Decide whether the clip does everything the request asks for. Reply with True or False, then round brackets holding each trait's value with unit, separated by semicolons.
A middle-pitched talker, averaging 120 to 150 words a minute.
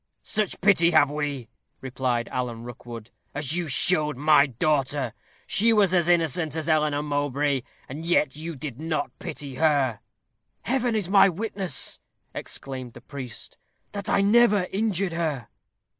True (150 Hz; 145 wpm)